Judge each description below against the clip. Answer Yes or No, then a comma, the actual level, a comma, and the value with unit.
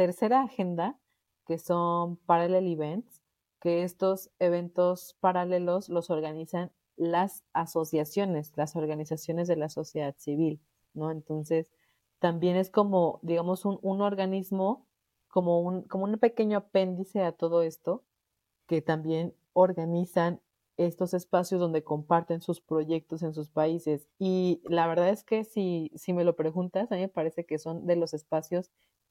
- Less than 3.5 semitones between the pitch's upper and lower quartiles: Yes, narrow, 2.4 semitones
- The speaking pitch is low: No, medium, 175 Hz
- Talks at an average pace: Yes, average, 140 wpm